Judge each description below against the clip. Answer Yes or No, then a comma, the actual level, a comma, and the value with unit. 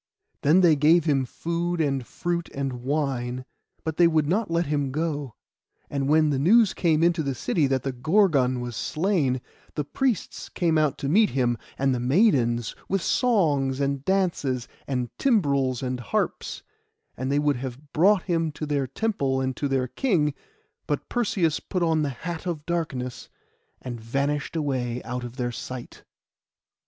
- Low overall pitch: No, medium, 145 Hz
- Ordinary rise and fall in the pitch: Yes, average, 4.5 semitones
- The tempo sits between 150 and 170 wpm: Yes, average, 165 wpm